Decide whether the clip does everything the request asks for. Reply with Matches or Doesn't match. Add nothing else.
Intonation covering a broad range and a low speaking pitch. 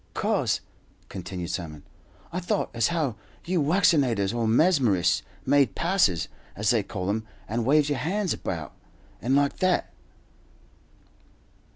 Matches